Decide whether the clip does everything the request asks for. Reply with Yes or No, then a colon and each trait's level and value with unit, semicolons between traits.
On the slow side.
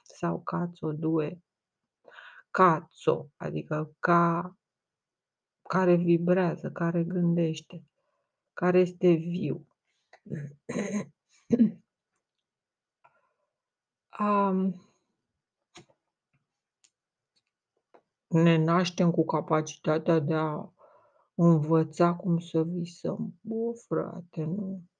Yes: slow, 65 wpm